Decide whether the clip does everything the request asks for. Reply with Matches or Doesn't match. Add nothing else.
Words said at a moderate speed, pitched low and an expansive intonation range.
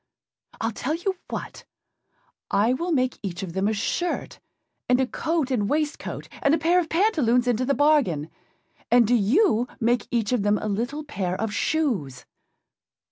Doesn't match